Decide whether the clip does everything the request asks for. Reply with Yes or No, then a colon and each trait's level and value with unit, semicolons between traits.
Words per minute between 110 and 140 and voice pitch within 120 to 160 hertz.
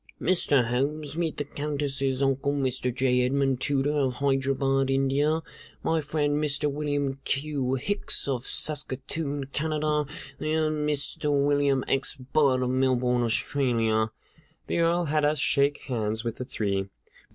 Yes: slow, 135 wpm; medium, 140 Hz